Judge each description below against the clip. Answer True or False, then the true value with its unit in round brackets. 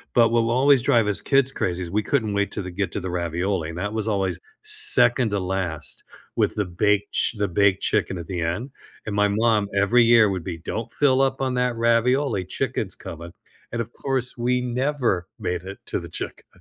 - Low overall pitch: True (105 Hz)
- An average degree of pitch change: True (4.7 semitones)